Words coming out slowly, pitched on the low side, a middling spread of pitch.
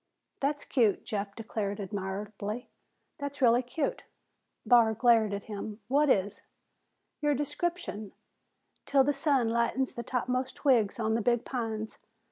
No: slow, 130 wpm; high, 235 Hz; average, 4.1 semitones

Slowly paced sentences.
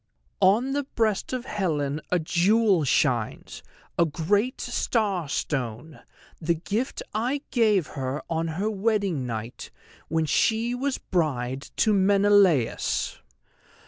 Yes: slow, 115 wpm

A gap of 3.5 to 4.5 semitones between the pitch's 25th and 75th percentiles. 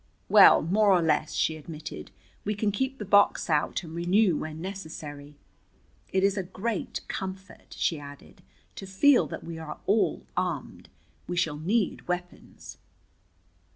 Yes: average, 4.1 semitones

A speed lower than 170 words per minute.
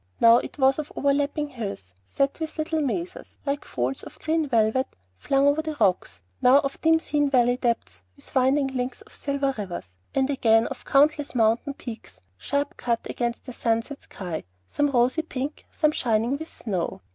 No: average, 180 wpm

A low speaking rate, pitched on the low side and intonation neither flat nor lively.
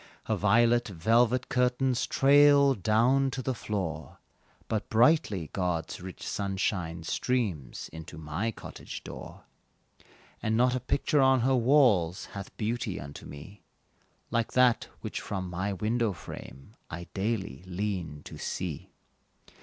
No: slow, 130 wpm; low, 105 Hz; wide, 5.7 semitones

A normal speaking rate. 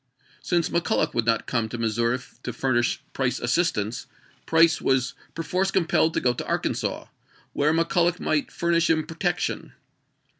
Yes: average, 155 wpm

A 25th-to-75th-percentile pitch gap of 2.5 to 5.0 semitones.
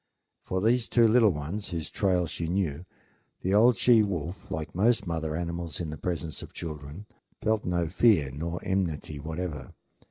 Yes: average, 4.3 semitones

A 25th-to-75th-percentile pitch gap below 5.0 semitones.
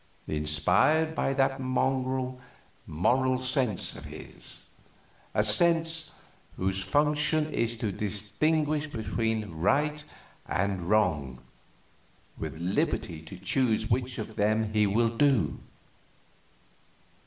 No: wide, 5.5 semitones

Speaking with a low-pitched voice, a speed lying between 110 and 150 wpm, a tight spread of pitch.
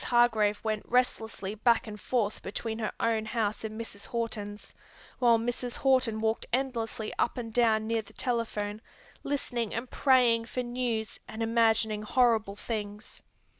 No: high, 225 Hz; average, 145 wpm; narrow, 1.9 semitones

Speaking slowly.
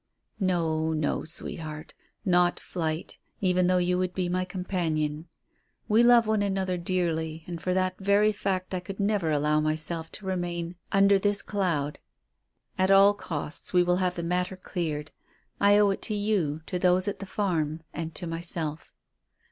No: average, 165 wpm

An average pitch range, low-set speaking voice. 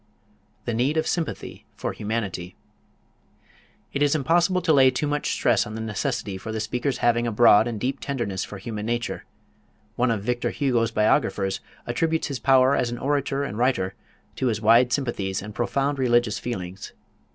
Yes: average, 4.2 semitones; low, 120 Hz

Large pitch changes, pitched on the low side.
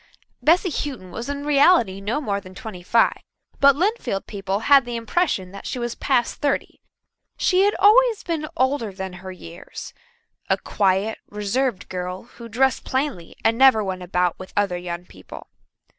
No: wide, 6.9 semitones; high, 225 Hz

